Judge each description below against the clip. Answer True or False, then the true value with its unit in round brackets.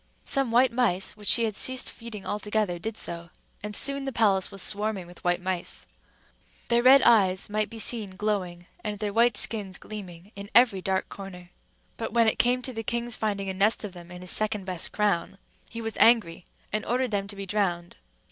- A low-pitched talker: False (210 Hz)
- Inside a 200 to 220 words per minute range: True (205 wpm)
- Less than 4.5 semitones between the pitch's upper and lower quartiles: True (3.4 semitones)